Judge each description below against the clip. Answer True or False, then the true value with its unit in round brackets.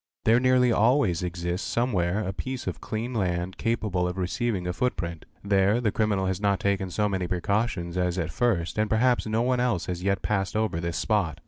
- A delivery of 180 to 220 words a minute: True (200 wpm)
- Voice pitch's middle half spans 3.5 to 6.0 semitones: True (4.1 semitones)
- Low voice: True (100 Hz)